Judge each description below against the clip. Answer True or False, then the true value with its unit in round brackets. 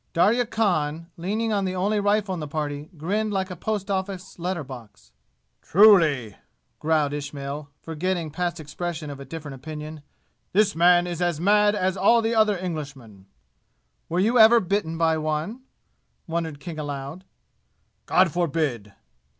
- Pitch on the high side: False (170 Hz)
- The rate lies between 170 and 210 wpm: False (150 wpm)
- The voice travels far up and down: False (4.6 semitones)